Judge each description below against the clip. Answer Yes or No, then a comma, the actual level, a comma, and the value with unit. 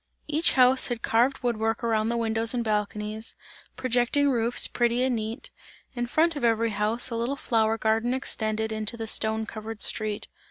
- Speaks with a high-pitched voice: Yes, high, 230 Hz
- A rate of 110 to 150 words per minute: No, average, 175 wpm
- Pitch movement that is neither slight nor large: No, narrow, 1.9 semitones